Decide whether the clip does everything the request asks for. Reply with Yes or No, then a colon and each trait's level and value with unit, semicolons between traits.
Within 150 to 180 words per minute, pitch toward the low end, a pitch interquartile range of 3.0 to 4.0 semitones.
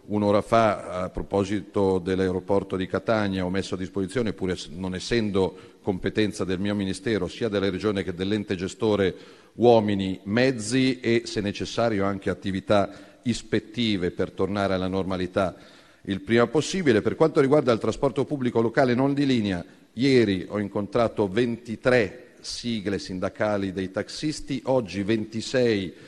No: average, 135 wpm; low, 105 Hz; average, 3.5 semitones